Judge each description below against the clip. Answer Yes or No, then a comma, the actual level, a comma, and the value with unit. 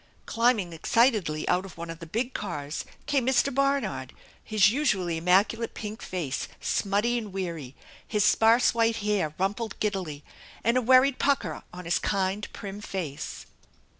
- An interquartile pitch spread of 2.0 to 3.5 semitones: No, average, 4.9 semitones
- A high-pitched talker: Yes, high, 205 Hz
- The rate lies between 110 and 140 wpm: No, average, 155 wpm